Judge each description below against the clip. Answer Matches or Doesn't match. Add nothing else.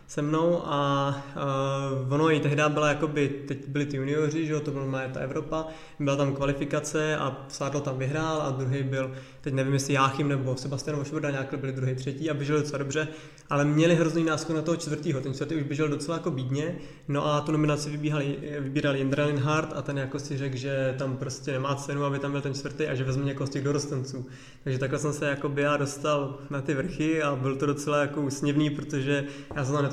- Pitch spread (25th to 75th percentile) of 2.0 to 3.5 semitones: Doesn't match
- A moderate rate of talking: Doesn't match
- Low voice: Doesn't match